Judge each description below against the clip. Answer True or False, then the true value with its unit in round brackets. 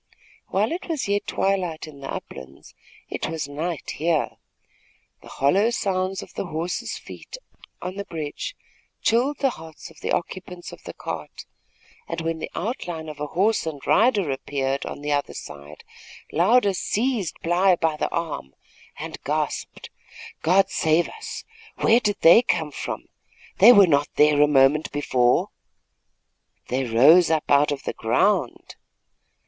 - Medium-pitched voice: True (165 Hz)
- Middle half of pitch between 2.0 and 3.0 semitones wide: False (5.0 semitones)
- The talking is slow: False (155 wpm)